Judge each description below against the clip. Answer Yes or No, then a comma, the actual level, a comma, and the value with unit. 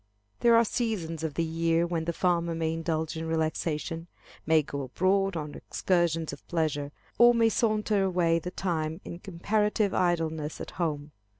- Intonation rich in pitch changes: No, average, 2.7 semitones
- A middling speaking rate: Yes, average, 165 wpm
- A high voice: No, medium, 165 Hz